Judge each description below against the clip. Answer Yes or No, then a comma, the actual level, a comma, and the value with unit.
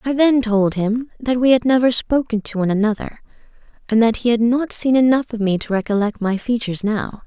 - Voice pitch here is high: Yes, high, 230 Hz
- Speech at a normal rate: No, fast, 215 wpm